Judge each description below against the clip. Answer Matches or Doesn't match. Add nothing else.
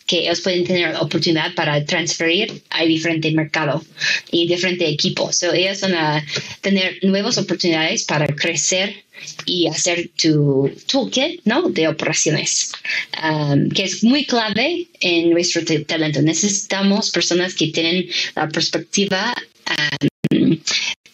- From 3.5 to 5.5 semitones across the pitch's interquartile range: Doesn't match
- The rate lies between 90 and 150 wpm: Matches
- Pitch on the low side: Doesn't match